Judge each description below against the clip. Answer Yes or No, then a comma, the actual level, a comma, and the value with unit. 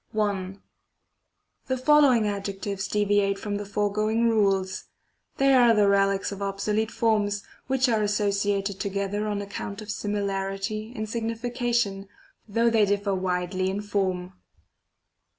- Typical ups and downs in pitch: No, narrow, 1.7 semitones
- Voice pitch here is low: No, high, 205 Hz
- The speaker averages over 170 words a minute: No, slow, 135 wpm